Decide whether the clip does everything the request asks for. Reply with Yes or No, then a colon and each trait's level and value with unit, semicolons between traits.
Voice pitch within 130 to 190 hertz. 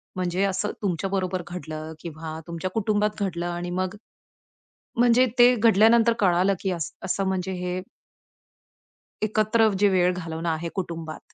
Yes: medium, 185 Hz